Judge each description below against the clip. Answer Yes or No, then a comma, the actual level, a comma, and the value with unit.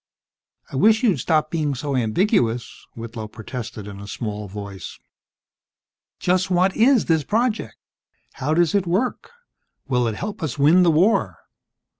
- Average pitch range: No, wide, 8.5 semitones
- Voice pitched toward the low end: No, medium, 155 Hz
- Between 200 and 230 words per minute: No, average, 145 wpm